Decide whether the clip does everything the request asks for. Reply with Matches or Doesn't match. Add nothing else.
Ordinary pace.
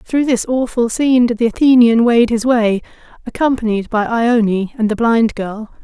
Matches